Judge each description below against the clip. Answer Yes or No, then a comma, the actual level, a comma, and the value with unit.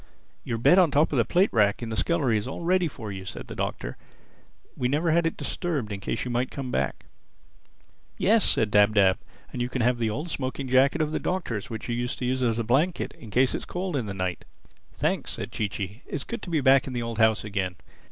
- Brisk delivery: Yes, fast, 250 wpm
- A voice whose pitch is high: No, low, 125 Hz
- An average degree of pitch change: No, wide, 5.7 semitones